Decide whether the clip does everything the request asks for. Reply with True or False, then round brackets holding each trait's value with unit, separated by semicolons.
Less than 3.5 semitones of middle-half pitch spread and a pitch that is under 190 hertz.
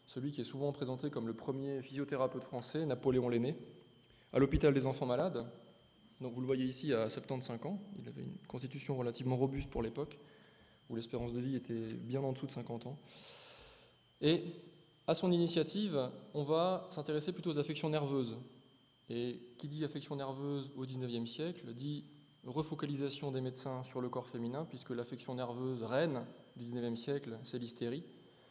True (3.0 semitones; 135 Hz)